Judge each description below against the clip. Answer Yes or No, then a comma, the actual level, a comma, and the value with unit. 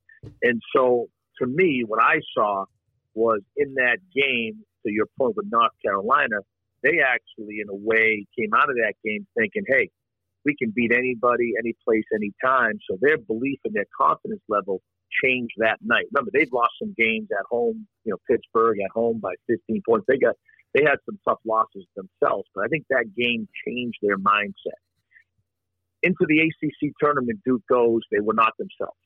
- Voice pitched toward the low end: Yes, low, 115 Hz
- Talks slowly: No, average, 185 wpm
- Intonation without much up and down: No, average, 3.0 semitones